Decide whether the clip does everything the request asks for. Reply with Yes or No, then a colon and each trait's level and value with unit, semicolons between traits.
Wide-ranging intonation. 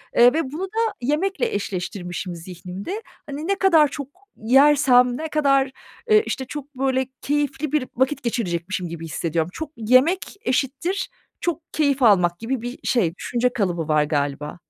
Yes: wide, 8.4 semitones